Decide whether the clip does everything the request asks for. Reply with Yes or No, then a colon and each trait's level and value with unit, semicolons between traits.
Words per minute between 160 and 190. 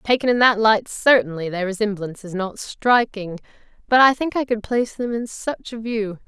No: average, 200 wpm